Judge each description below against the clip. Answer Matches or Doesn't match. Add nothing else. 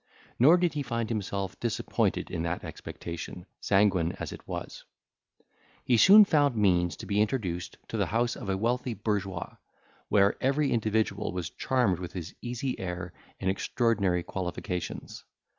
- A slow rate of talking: Doesn't match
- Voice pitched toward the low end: Matches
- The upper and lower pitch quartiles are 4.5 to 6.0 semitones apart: Matches